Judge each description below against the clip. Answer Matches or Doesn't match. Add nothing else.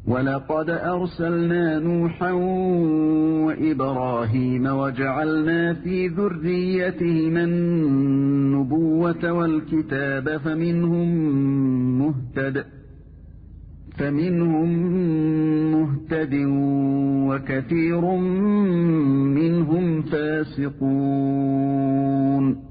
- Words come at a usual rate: Doesn't match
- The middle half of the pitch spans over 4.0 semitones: Doesn't match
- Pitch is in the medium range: Matches